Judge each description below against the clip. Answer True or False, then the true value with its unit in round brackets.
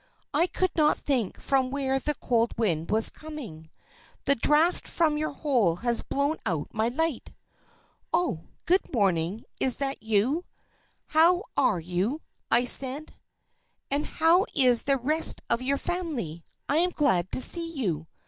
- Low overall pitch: False (270 Hz)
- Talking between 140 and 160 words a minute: True (150 wpm)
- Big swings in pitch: True (6.1 semitones)